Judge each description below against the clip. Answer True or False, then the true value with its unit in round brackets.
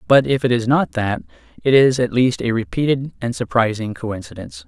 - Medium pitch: False (120 Hz)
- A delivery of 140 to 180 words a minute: False (195 wpm)